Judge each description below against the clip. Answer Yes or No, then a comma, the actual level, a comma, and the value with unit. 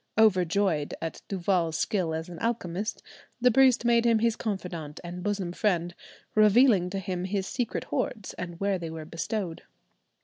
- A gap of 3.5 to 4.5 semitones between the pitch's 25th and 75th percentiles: Yes, average, 4.1 semitones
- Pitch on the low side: No, high, 190 Hz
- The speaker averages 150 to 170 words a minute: Yes, average, 160 wpm